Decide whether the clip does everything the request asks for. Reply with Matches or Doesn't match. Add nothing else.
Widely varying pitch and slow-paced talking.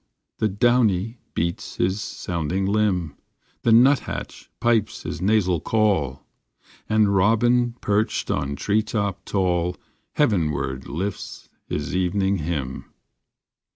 Doesn't match